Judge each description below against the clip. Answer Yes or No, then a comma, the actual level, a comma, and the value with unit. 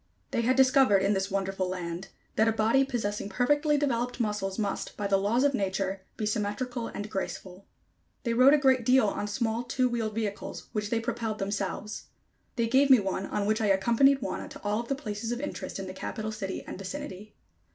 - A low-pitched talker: No, high, 215 Hz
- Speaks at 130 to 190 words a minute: No, fast, 205 wpm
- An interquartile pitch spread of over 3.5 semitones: Yes, average, 3.9 semitones